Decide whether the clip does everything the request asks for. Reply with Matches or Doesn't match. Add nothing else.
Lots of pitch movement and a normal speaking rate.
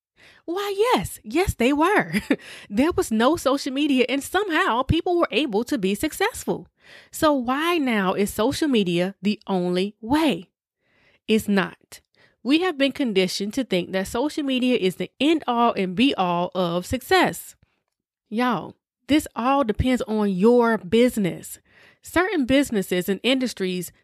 Matches